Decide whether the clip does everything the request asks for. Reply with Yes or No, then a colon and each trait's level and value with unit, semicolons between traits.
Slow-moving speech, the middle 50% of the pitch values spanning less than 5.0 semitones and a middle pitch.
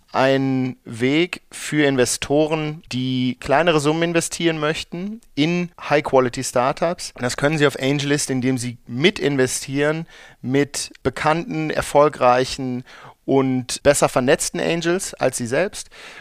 Yes: slow, 120 wpm; average, 3.8 semitones; medium, 145 Hz